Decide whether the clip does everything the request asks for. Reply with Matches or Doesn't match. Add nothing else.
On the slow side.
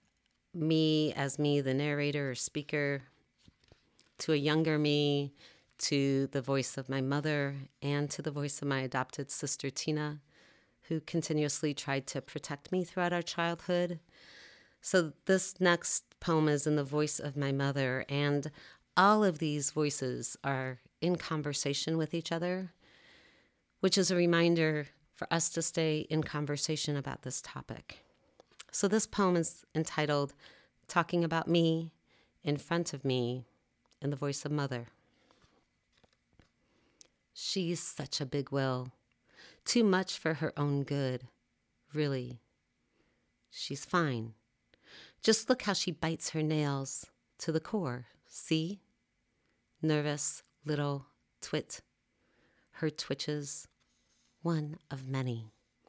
Matches